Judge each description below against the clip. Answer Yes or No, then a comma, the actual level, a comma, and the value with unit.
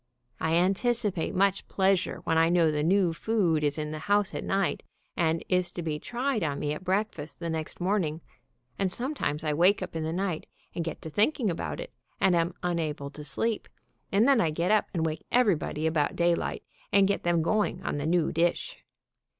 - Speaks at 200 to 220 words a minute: Yes, fast, 205 wpm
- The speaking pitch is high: No, medium, 175 Hz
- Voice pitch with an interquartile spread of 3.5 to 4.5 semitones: Yes, average, 3.8 semitones